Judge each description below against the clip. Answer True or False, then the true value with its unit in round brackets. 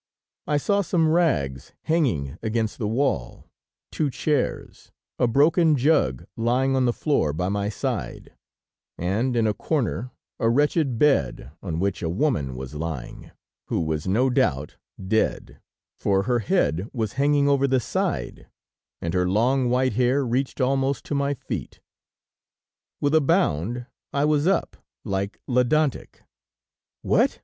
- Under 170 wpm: True (140 wpm)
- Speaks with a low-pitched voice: True (125 Hz)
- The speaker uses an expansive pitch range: True (6.8 semitones)